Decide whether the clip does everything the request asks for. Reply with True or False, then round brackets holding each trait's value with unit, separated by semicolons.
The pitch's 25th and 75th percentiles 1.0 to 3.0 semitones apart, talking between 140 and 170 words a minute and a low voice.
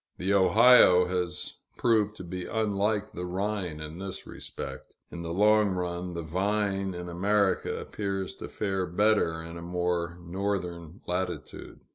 True (2.7 semitones; 145 wpm; 95 Hz)